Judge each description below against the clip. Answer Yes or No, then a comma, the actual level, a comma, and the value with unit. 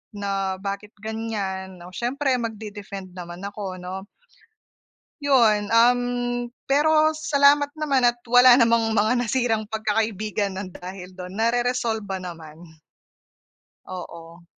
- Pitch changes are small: No, average, 4.2 semitones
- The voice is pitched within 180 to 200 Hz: No, high, 215 Hz